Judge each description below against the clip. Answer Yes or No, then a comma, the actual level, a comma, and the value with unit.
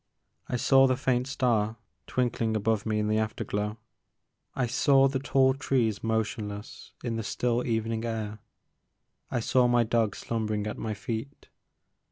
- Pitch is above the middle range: No, low, 115 Hz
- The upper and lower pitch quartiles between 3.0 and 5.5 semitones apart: No, narrow, 2.6 semitones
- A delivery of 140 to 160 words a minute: Yes, average, 150 wpm